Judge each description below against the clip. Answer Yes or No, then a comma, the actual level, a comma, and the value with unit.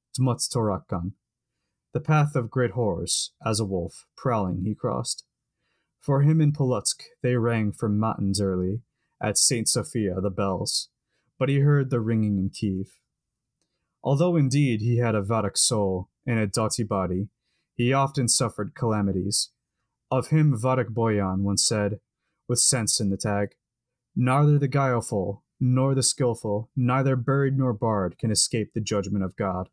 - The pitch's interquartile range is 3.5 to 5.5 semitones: Yes, average, 4.1 semitones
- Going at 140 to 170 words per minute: Yes, average, 150 wpm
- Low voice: Yes, low, 115 Hz